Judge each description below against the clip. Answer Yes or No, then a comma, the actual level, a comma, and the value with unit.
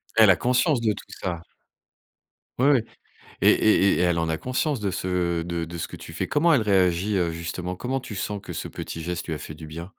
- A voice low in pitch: Yes, very low, 90 Hz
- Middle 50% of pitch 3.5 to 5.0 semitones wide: Yes, average, 4.5 semitones